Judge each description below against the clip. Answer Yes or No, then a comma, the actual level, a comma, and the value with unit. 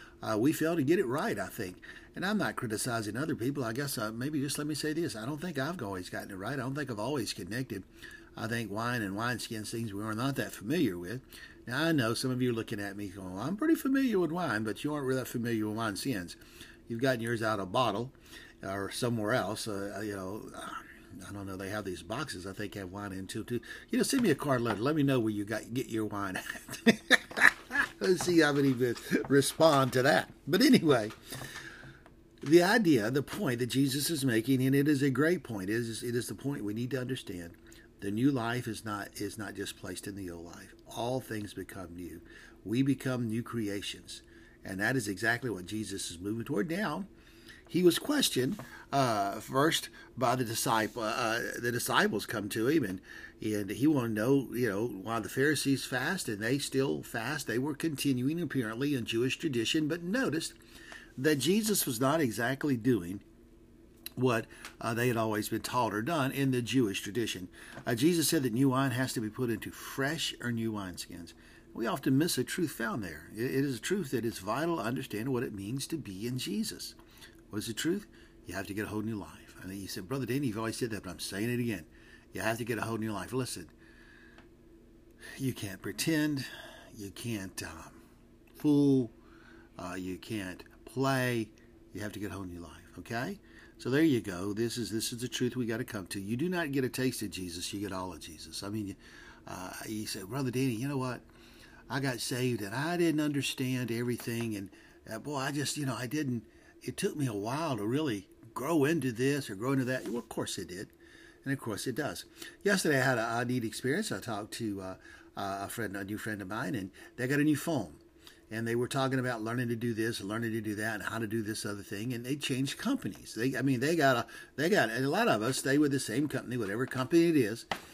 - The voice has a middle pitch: No, low, 115 Hz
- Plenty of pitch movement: No, average, 4.2 semitones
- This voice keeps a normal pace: No, fast, 225 wpm